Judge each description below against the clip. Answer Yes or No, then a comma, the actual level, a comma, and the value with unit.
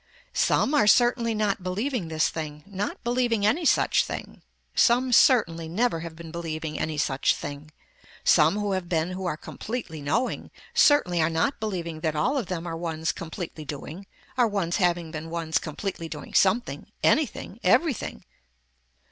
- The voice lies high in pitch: No, medium, 175 Hz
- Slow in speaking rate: No, average, 160 wpm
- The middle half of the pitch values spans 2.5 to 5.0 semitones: No, wide, 5.5 semitones